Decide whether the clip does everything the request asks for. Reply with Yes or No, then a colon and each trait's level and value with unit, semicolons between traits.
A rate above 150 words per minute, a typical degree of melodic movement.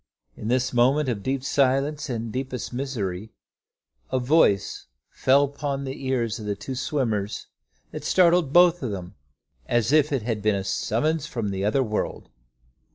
Yes: average, 160 wpm; average, 4.4 semitones